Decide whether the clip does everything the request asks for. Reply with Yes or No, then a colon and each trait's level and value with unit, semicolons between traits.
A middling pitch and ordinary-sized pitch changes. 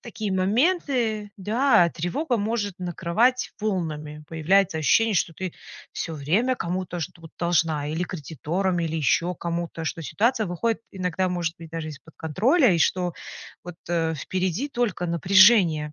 Yes: medium, 180 Hz; average, 4.5 semitones